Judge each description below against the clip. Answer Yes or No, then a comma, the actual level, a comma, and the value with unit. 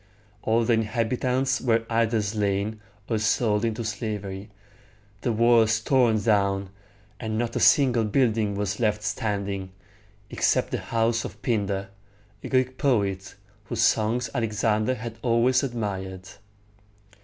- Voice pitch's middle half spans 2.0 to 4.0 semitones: Yes, narrow, 2.5 semitones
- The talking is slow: Yes, slow, 125 wpm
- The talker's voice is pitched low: Yes, low, 110 Hz